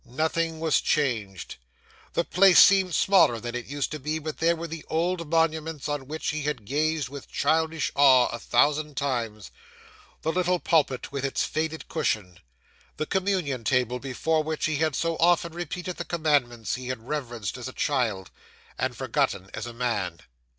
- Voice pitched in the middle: Yes, medium, 150 Hz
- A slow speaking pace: No, average, 170 wpm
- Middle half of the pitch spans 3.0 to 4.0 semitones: No, average, 4.6 semitones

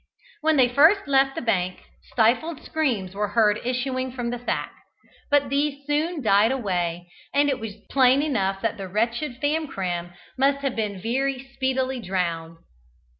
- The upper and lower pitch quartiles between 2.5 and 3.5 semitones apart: No, wide, 5.6 semitones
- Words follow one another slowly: No, average, 155 wpm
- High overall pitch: Yes, very high, 250 Hz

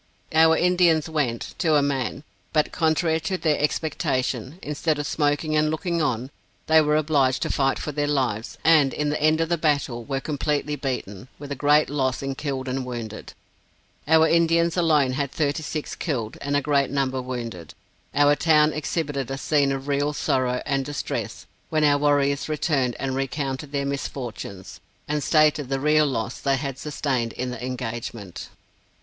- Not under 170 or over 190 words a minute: Yes, average, 175 wpm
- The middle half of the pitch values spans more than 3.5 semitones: No, narrow, 2.6 semitones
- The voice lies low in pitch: No, medium, 145 Hz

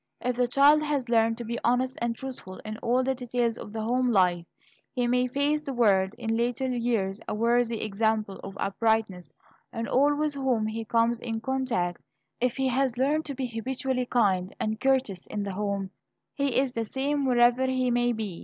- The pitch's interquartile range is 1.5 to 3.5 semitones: Yes, average, 3.1 semitones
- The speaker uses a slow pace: No, average, 195 wpm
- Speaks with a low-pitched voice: No, high, 240 Hz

